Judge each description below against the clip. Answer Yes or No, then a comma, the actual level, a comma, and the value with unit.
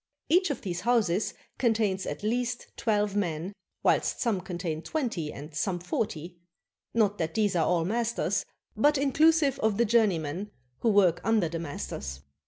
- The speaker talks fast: No, average, 160 wpm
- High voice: Yes, high, 205 Hz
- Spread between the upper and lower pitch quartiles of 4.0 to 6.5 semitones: Yes, wide, 5.4 semitones